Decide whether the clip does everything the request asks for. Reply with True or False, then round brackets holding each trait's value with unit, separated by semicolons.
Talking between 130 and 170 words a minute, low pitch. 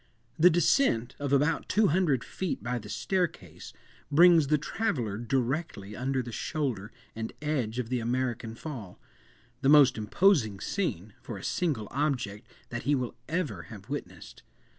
True (145 wpm; 130 Hz)